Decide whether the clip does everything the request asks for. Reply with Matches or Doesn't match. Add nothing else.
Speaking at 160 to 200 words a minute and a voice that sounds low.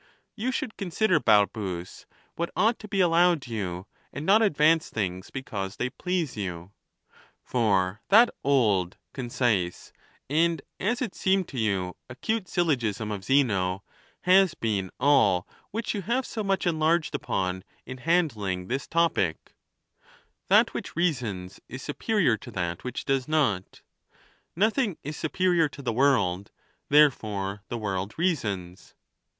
Doesn't match